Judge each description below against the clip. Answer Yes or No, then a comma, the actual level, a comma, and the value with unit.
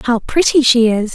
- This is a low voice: No, high, 245 Hz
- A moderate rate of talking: No, fast, 210 wpm